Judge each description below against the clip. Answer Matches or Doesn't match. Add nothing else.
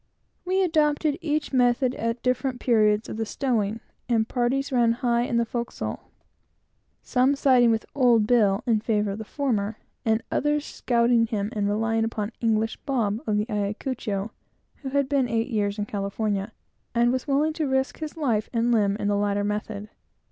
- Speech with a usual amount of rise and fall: Matches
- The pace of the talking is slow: Doesn't match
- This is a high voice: Matches